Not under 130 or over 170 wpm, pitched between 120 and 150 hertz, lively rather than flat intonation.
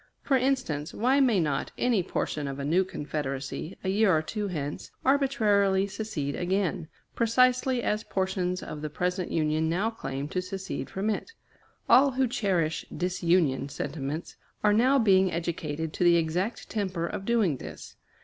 No: average, 160 wpm; medium, 185 Hz; wide, 5.7 semitones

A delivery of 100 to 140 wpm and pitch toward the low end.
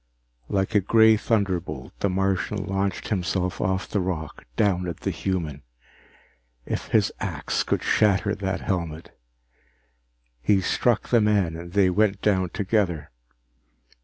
Yes: slow, 135 wpm; very low, 95 Hz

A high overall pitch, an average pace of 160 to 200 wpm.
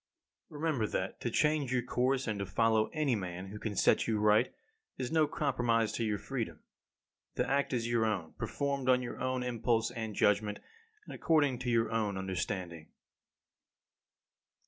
No: low, 115 Hz; average, 170 wpm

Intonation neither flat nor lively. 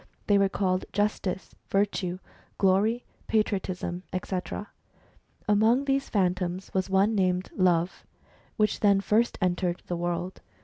No: narrow, 2.3 semitones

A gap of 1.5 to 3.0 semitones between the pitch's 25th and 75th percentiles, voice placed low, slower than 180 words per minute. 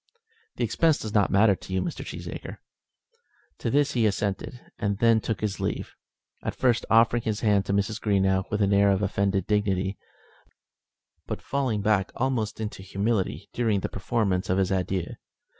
Yes: average, 2.7 semitones; low, 105 Hz; average, 170 wpm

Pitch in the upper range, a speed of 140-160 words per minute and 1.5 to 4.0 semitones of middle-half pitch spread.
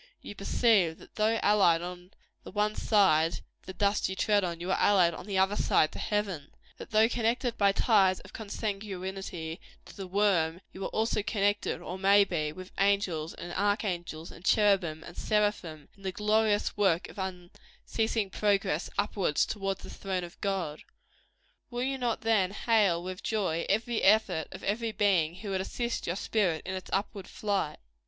No: high, 195 Hz; average, 175 wpm; average, 2.9 semitones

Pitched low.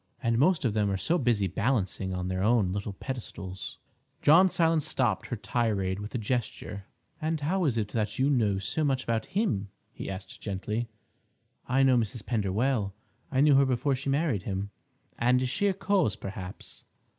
Yes: low, 115 Hz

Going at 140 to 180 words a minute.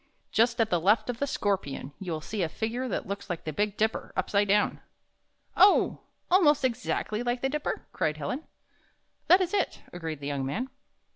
No: average, 195 wpm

